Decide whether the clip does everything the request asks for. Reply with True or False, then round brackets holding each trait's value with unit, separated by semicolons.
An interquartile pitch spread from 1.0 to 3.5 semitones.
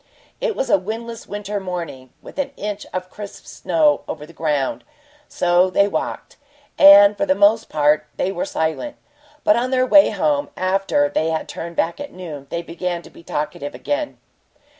False (5.2 semitones)